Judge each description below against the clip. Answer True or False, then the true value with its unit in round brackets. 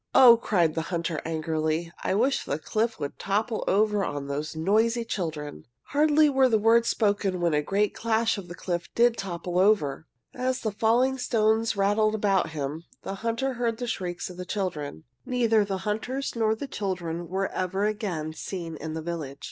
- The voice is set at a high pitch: True (195 Hz)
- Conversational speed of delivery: True (180 wpm)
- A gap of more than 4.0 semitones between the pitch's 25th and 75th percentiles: True (5.3 semitones)